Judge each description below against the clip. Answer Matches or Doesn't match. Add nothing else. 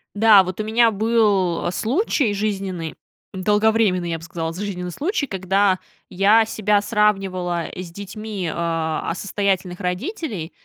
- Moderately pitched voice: Doesn't match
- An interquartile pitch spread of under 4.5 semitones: Matches